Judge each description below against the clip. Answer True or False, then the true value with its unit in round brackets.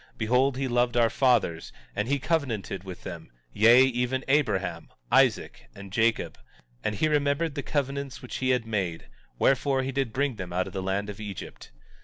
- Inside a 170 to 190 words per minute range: True (180 wpm)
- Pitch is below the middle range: True (120 Hz)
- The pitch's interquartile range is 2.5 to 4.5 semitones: False (5.0 semitones)